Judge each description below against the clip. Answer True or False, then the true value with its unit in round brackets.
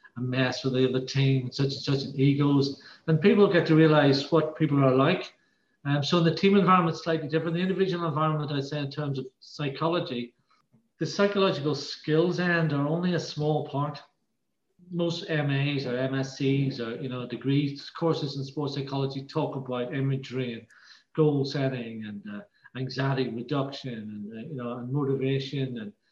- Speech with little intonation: False (3.2 semitones)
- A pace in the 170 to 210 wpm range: True (175 wpm)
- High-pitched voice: False (140 Hz)